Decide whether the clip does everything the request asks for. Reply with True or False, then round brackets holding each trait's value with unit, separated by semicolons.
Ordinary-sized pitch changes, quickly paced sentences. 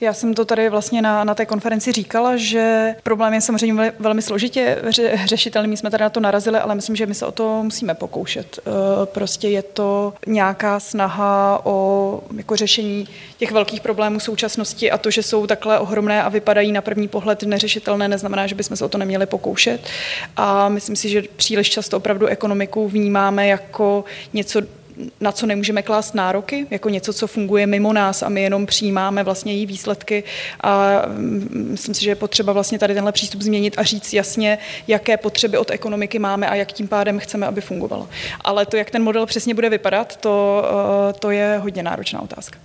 False (1.4 semitones; 190 wpm)